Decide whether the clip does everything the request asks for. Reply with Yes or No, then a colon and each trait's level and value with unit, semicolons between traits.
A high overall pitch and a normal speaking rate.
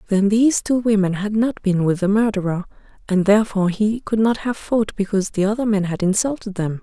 No: high, 205 Hz; fast, 210 wpm